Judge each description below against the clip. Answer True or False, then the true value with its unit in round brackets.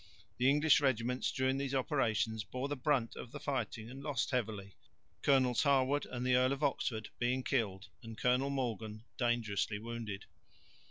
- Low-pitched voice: True (125 Hz)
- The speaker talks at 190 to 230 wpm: False (160 wpm)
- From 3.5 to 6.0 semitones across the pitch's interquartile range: False (3.1 semitones)